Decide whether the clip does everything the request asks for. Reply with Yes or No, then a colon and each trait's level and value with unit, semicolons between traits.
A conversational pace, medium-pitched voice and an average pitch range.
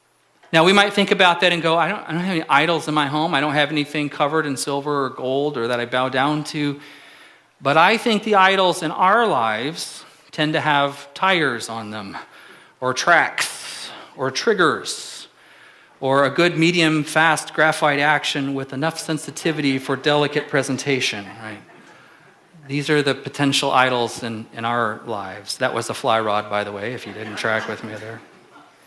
Yes: average, 185 wpm; medium, 145 Hz; average, 4.0 semitones